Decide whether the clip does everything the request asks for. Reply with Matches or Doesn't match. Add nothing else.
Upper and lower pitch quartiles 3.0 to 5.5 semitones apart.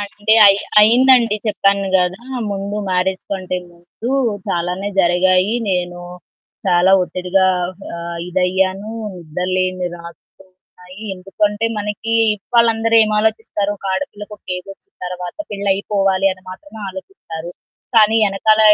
Doesn't match